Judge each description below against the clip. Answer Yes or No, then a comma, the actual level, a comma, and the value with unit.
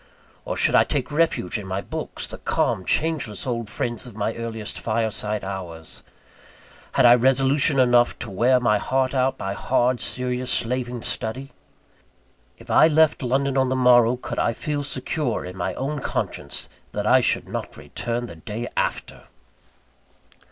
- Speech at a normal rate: Yes, average, 160 wpm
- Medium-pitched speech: No, low, 120 Hz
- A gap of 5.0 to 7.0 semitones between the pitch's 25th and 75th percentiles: No, average, 3.3 semitones